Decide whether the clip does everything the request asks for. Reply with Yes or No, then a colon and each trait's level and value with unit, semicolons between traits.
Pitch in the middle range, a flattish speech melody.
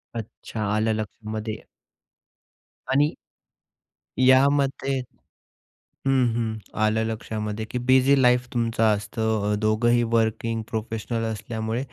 No: low, 115 Hz; narrow, 2.2 semitones